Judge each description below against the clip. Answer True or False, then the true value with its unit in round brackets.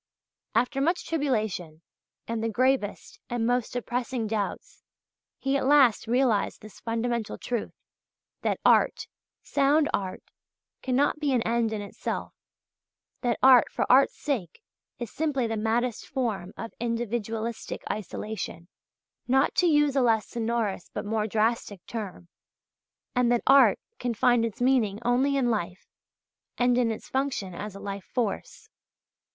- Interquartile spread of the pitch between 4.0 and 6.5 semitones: False (3.3 semitones)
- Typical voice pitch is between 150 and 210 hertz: False (235 Hz)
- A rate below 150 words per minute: True (140 wpm)